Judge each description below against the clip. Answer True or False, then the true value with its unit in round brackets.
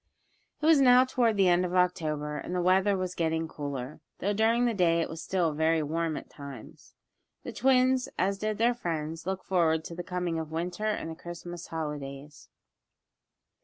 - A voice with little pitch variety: False (3.9 semitones)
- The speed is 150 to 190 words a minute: True (185 wpm)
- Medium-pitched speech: True (175 Hz)